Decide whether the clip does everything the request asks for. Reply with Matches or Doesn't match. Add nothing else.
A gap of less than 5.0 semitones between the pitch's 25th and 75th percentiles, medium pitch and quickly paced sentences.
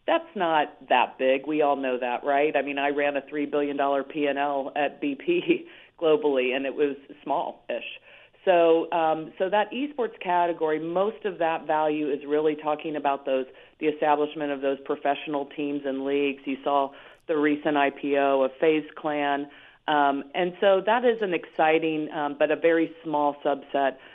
Doesn't match